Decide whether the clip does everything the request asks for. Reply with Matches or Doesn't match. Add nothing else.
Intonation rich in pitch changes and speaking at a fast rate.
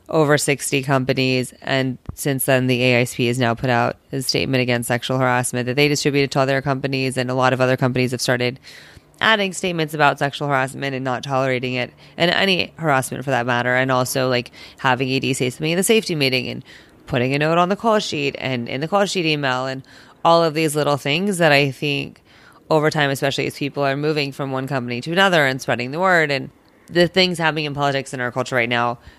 Doesn't match